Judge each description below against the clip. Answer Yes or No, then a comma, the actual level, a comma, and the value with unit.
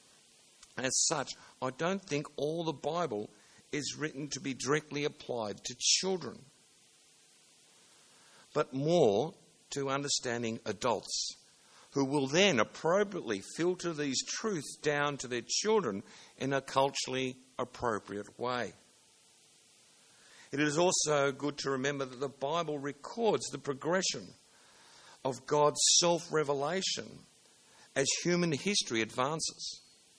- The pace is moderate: No, slow, 115 wpm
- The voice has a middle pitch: Yes, medium, 145 Hz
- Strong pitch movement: No, average, 3.9 semitones